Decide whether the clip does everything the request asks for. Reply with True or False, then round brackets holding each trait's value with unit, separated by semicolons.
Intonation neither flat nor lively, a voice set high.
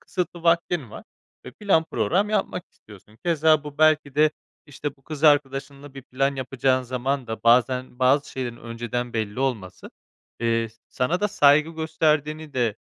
False (4.0 semitones; 140 Hz)